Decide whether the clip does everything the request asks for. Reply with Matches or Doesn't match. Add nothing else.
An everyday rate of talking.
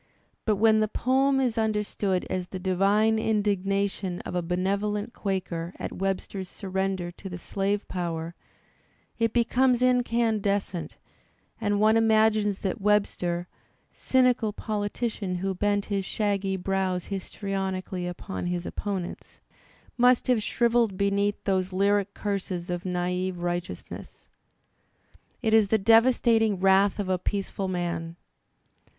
Doesn't match